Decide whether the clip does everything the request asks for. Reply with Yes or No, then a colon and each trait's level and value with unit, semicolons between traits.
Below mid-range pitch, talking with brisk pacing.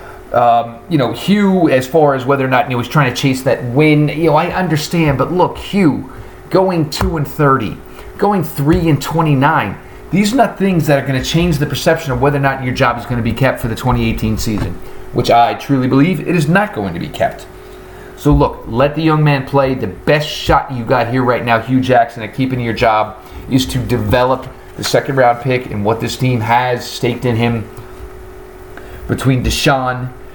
Yes: low, 130 Hz; fast, 210 wpm